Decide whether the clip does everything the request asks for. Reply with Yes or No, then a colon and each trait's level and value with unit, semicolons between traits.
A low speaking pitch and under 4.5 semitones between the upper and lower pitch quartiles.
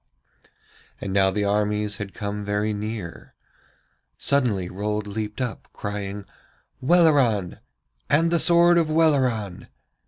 No: low, 105 Hz; wide, 5.4 semitones